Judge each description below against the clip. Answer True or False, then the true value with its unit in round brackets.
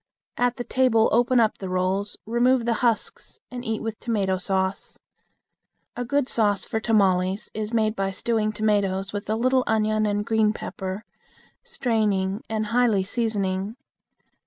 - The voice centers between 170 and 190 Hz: False (215 Hz)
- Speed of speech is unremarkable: True (150 wpm)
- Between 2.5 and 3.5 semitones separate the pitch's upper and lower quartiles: True (2.9 semitones)